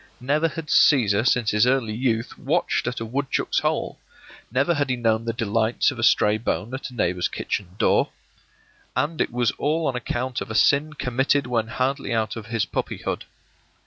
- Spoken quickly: No, average, 185 wpm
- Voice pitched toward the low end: Yes, low, 120 Hz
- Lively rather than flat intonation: No, average, 3.4 semitones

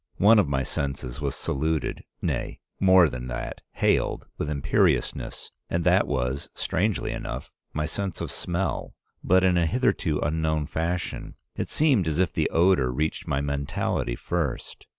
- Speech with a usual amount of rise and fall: Yes, average, 4.4 semitones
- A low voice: Yes, very low, 80 Hz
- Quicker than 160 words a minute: No, average, 150 wpm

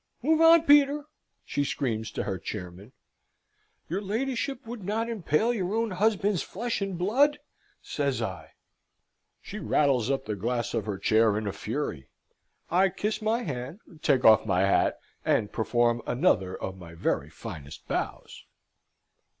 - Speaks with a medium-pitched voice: Yes, medium, 145 Hz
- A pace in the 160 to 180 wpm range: No, average, 150 wpm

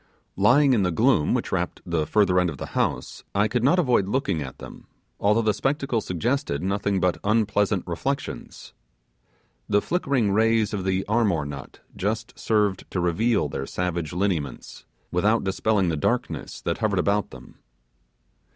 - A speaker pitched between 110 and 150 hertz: No, low, 100 Hz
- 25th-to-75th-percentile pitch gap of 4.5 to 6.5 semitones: No, average, 4.0 semitones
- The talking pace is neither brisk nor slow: Yes, average, 160 wpm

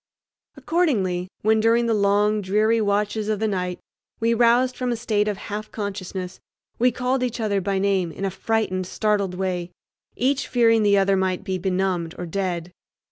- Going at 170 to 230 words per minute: Yes, average, 175 wpm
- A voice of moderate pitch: No, high, 205 Hz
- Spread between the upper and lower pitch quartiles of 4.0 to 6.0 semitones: No, average, 3.1 semitones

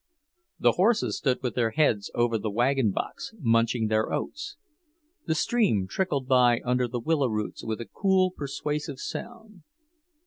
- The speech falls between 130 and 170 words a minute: Yes, average, 150 wpm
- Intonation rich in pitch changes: Yes, wide, 7.4 semitones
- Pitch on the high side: No, low, 130 Hz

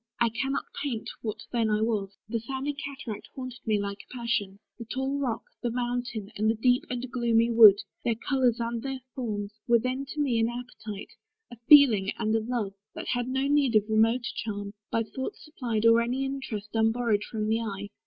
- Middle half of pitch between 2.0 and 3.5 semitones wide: Yes, average, 2.8 semitones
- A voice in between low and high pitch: No, high, 235 Hz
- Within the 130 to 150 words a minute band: No, average, 200 wpm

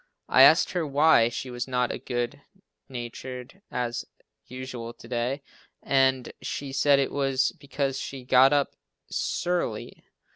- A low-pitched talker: Yes, low, 130 Hz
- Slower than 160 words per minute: Yes, average, 140 wpm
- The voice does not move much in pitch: Yes, narrow, 2.2 semitones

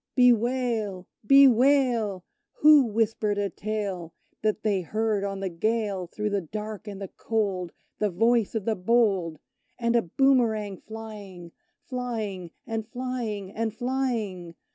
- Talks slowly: Yes, slow, 130 wpm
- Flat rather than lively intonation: No, average, 3.2 semitones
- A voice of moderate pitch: No, high, 215 Hz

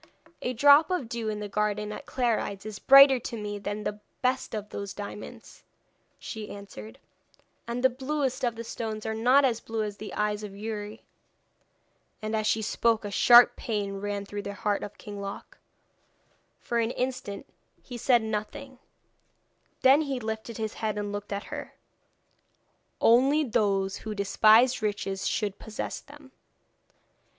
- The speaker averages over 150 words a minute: Yes, average, 160 wpm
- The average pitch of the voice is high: Yes, high, 220 Hz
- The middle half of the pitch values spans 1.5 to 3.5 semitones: Yes, average, 3.0 semitones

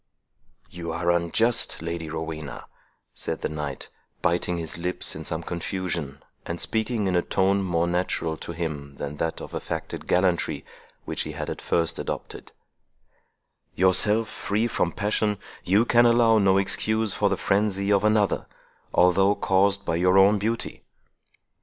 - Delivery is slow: No, average, 150 wpm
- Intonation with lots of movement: No, average, 3.6 semitones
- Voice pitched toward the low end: Yes, very low, 95 Hz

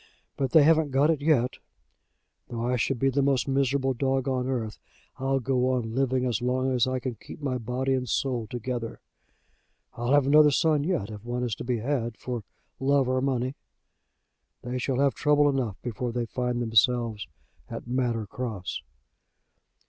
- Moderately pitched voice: No, low, 125 Hz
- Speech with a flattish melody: Yes, narrow, 2.1 semitones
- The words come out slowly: No, average, 175 wpm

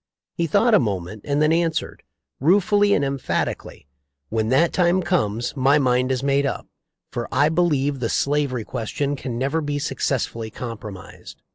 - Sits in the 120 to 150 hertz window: Yes, medium, 140 Hz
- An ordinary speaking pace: Yes, average, 155 wpm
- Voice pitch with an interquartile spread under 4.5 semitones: No, average, 4.8 semitones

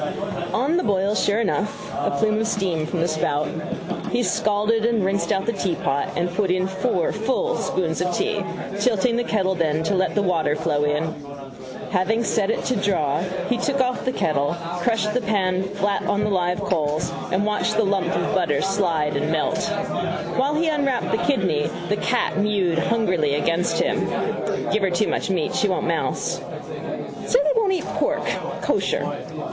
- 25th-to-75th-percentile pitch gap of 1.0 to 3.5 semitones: No, average, 4.7 semitones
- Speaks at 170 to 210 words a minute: Yes, average, 180 wpm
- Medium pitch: No, high, 195 Hz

